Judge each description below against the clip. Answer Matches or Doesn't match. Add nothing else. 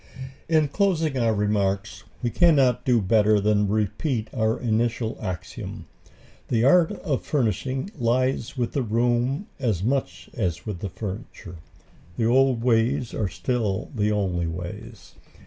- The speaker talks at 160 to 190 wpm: Doesn't match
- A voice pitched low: Matches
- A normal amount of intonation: Matches